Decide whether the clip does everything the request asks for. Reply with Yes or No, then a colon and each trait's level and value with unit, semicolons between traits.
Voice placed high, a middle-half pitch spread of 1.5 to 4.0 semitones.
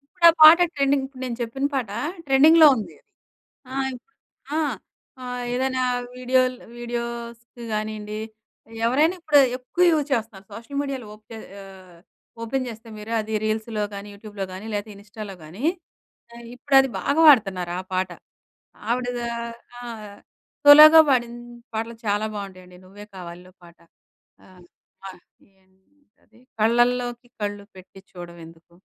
No: high, 230 Hz; average, 4.7 semitones